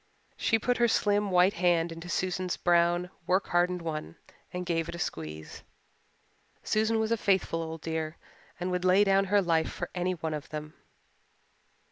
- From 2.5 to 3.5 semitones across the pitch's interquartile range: Yes, average, 2.8 semitones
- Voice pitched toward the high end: No, medium, 175 Hz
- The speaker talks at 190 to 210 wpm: No, average, 170 wpm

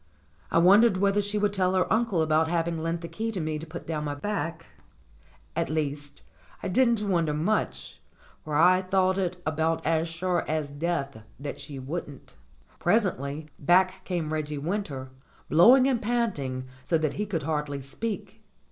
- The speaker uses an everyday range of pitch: Yes, average, 4.2 semitones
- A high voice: No, medium, 165 Hz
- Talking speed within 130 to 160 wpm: No, average, 170 wpm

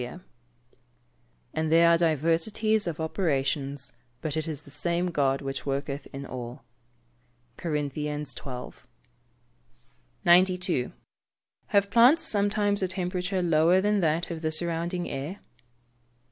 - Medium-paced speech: No, slow, 120 wpm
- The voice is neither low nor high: Yes, medium, 165 Hz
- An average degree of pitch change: Yes, average, 4.2 semitones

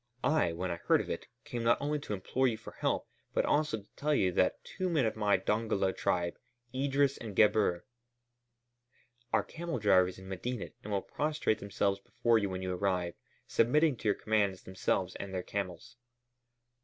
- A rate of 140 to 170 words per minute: No, average, 180 wpm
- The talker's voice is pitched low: Yes, low, 105 Hz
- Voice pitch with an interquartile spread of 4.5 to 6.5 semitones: Yes, wide, 5.4 semitones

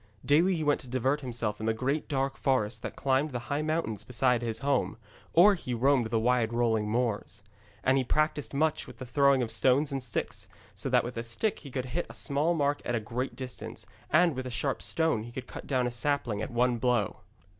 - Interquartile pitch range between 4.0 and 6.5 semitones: No, average, 3.3 semitones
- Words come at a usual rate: No, fast, 225 wpm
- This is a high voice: No, low, 130 Hz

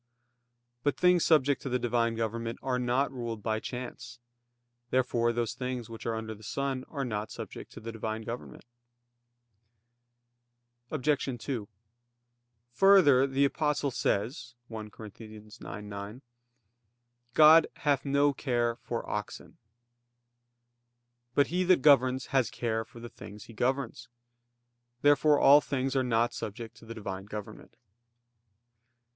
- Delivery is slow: Yes, slow, 130 wpm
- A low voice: Yes, low, 120 Hz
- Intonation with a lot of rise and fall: No, average, 3.6 semitones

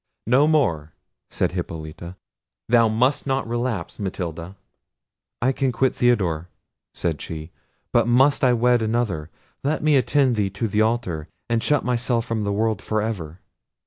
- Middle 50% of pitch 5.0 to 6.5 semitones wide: Yes, wide, 5.5 semitones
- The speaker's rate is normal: Yes, average, 150 wpm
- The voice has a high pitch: No, low, 115 Hz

